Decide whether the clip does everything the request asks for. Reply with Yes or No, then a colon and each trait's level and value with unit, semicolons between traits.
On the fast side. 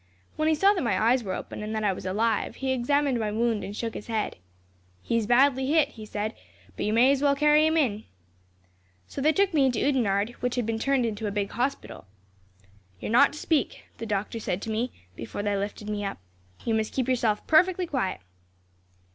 Yes: fast, 220 wpm